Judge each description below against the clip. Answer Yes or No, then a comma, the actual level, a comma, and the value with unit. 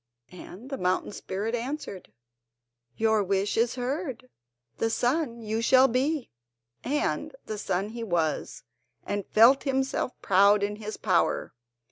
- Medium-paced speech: No, slow, 130 wpm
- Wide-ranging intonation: No, average, 4.2 semitones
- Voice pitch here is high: Yes, high, 225 Hz